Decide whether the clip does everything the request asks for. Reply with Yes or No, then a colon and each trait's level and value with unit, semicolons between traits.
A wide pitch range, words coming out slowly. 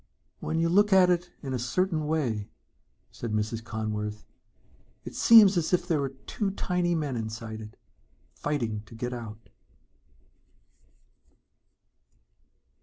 Yes: wide, 7.8 semitones; slow, 125 wpm